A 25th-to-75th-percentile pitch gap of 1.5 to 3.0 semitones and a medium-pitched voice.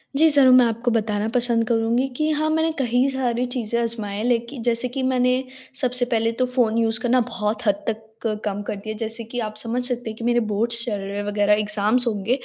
No: narrow, 2.5 semitones; high, 235 Hz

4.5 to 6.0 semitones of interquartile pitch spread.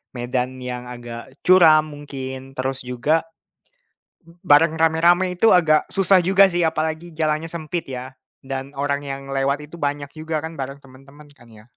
No: average, 3.5 semitones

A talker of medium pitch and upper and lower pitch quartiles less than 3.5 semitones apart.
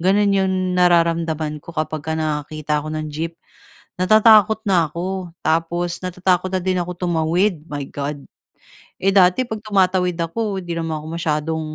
Yes: medium, 170 Hz; average, 3.0 semitones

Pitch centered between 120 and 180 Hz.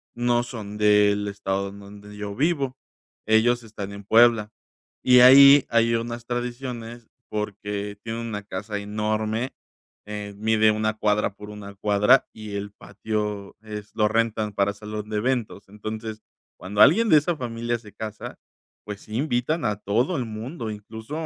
No: low, 110 Hz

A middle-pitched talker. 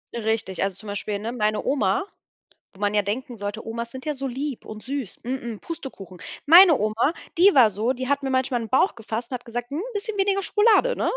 No: high, 245 Hz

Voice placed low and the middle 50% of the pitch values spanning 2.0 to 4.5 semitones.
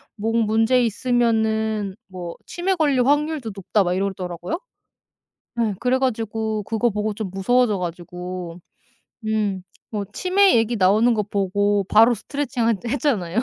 No: high, 220 Hz; average, 3.8 semitones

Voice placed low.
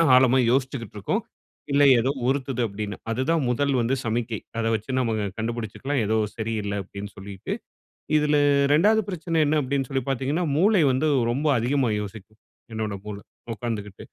Yes: low, 125 Hz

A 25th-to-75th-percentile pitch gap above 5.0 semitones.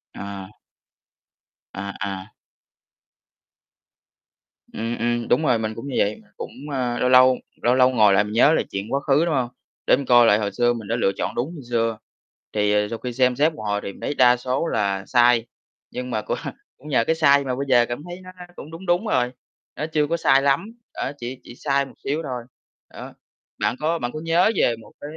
No: average, 3.8 semitones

